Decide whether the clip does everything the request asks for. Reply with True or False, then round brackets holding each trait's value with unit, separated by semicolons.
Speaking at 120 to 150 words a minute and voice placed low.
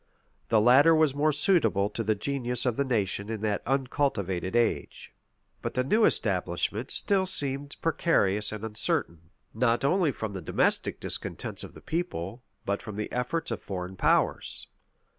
False (160 wpm; 120 Hz)